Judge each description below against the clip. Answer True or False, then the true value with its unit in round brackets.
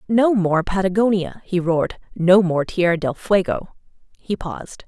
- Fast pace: False (150 wpm)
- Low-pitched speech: False (185 Hz)